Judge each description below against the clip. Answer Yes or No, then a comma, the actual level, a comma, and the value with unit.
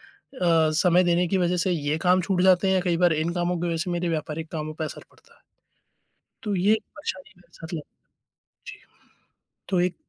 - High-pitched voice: No, medium, 175 Hz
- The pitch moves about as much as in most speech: No, narrow, 2.0 semitones